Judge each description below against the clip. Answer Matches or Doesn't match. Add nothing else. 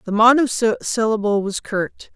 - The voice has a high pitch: Matches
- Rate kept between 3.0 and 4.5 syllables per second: Matches